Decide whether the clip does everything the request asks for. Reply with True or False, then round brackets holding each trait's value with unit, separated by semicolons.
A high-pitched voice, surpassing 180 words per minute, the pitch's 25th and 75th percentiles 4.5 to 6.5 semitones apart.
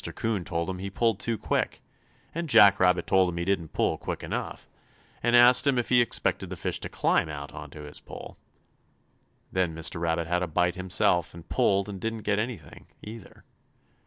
False (95 Hz; 190 wpm; 4.8 semitones)